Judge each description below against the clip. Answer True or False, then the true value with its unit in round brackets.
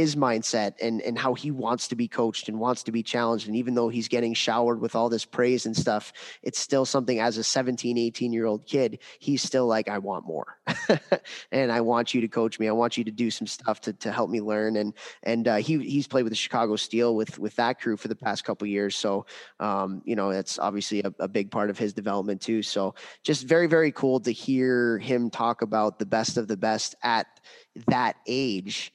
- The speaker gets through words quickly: True (235 wpm)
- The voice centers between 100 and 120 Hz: True (115 Hz)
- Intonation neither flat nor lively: False (2.3 semitones)